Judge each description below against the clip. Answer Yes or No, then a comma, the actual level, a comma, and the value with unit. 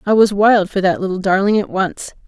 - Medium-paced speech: No, fast, 240 wpm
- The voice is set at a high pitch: Yes, high, 195 Hz